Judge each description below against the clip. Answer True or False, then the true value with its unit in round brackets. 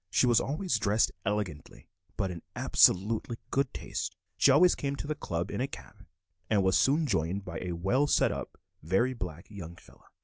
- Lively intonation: True (7.1 semitones)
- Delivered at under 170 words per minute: False (190 wpm)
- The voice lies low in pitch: True (105 Hz)